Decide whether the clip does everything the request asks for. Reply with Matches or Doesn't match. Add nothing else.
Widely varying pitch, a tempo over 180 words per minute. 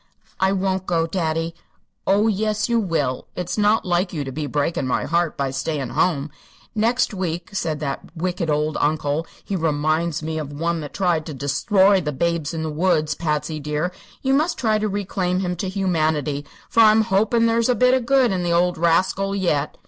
Doesn't match